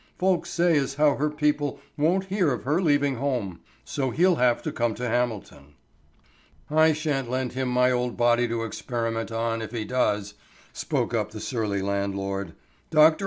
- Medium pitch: No, low, 125 Hz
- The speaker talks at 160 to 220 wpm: Yes, average, 170 wpm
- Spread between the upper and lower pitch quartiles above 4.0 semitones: Yes, average, 4.7 semitones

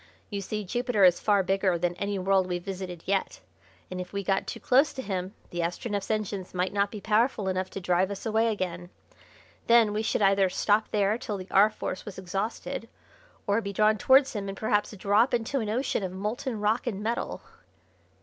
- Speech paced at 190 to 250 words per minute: Yes, average, 200 wpm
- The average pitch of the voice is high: Yes, high, 200 Hz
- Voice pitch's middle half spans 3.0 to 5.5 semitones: No, narrow, 2.4 semitones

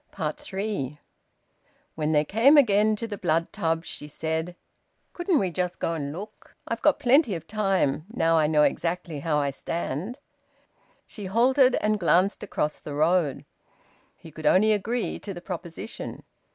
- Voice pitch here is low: No, medium, 180 Hz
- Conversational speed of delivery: Yes, average, 160 wpm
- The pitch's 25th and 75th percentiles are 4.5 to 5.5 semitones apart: Yes, average, 5.2 semitones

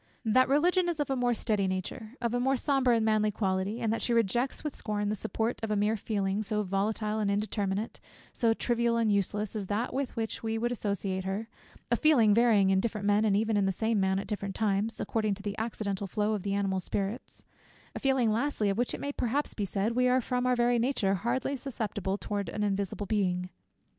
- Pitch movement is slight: No, average, 3.0 semitones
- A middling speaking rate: No, fast, 225 wpm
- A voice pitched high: Yes, high, 215 Hz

